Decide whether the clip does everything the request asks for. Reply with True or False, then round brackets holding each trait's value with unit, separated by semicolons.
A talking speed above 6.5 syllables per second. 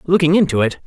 True (6.8 syllables/s)